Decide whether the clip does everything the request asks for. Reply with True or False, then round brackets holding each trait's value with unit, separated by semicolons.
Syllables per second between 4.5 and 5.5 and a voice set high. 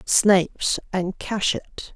True (4.6 syllables/s; 195 Hz)